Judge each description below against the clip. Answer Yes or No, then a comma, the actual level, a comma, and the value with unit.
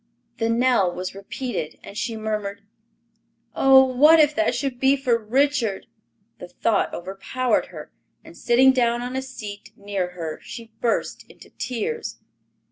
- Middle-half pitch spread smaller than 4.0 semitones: No, average, 4.6 semitones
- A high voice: Yes, high, 235 Hz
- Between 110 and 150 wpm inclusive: Yes, average, 145 wpm